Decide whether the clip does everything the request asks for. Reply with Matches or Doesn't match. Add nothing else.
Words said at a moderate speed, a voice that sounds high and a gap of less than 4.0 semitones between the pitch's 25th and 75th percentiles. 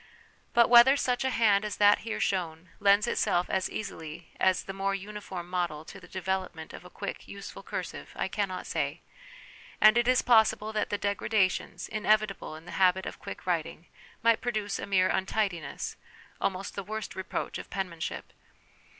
Matches